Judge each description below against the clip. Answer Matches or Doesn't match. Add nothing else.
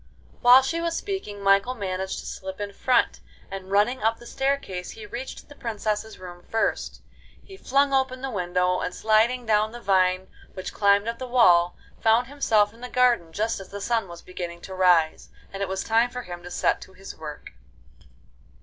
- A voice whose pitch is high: Matches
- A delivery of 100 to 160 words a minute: Doesn't match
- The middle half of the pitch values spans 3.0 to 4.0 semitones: Doesn't match